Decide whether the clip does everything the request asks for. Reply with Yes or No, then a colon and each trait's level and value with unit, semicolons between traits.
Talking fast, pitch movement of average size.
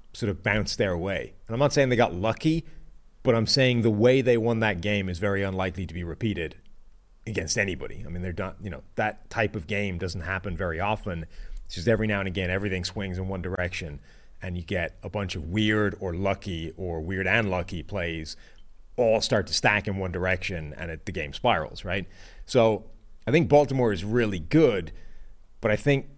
Yes: fast, 210 wpm; average, 3.7 semitones